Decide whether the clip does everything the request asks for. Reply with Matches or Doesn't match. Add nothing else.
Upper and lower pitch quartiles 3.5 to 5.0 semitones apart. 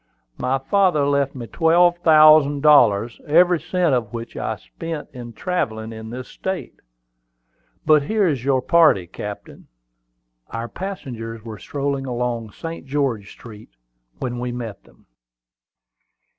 Doesn't match